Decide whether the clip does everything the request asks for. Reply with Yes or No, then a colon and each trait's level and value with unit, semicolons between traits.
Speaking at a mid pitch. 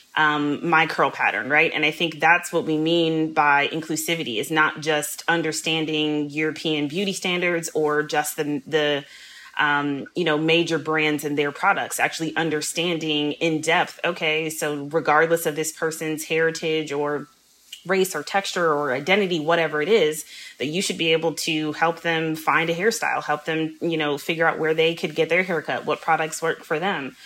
Yes: medium, 160 Hz